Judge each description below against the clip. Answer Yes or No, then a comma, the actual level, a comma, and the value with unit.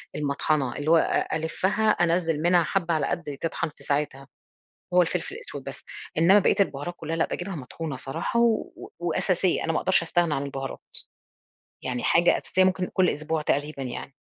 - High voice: No, medium, 165 Hz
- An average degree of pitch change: Yes, average, 3.7 semitones